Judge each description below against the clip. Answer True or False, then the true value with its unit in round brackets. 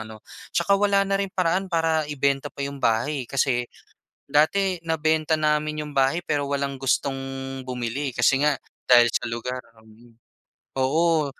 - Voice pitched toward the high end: False (145 Hz)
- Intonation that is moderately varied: True (3.7 semitones)